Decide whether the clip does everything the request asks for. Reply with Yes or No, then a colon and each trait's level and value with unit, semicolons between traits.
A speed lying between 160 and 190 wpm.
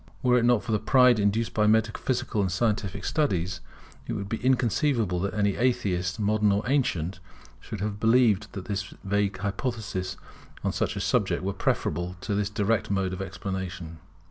Yes: average, 170 wpm